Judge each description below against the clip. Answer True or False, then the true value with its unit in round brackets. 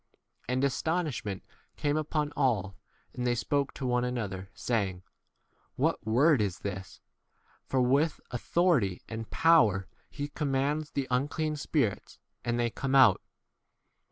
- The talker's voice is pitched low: True (125 Hz)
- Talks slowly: True (130 wpm)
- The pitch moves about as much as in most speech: True (4.9 semitones)